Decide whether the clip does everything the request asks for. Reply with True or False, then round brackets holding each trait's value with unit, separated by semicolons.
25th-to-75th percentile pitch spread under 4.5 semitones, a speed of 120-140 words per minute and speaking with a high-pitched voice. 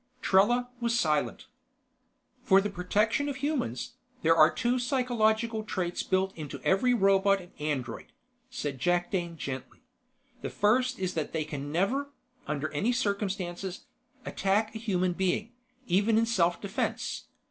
False (4.9 semitones; 135 wpm; 195 Hz)